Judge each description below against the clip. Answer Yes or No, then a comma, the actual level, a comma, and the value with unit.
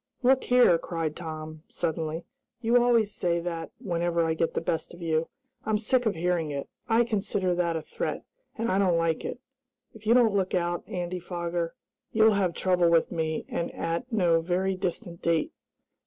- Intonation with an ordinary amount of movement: Yes, average, 4.0 semitones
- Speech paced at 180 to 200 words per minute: Yes, average, 185 wpm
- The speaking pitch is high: No, medium, 175 Hz